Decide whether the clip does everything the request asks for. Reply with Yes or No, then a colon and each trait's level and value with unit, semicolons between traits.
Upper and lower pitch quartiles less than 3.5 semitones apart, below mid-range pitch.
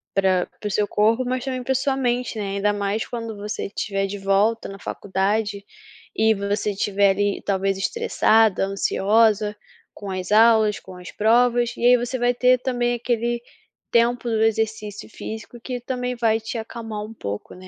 No: average, 3.1 semitones; high, 220 Hz